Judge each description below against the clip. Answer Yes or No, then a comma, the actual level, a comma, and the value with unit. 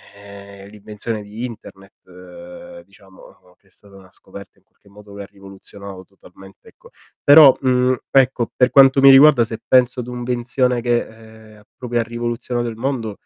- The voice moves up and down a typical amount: Yes, average, 4.0 semitones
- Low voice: Yes, low, 115 Hz